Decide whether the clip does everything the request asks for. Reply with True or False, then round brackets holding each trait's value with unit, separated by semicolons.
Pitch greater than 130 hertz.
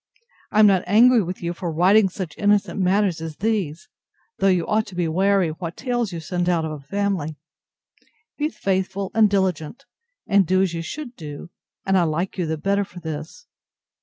True (185 Hz)